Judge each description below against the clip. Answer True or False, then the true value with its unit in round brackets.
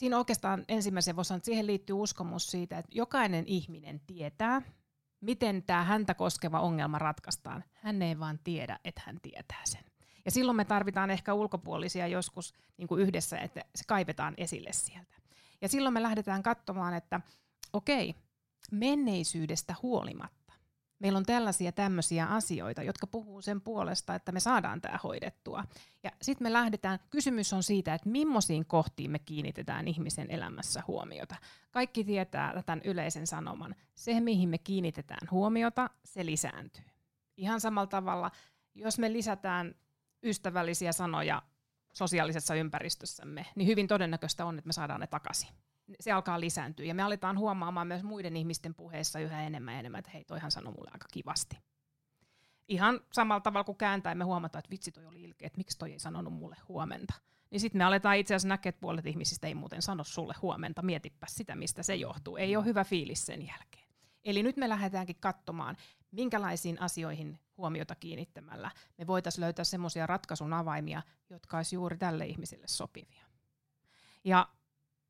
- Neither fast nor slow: False (160 wpm)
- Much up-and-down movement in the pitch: False (3.9 semitones)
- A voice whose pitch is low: False (180 Hz)